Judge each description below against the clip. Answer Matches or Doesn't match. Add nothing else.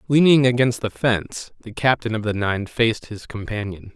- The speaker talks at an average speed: Matches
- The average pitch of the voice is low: Matches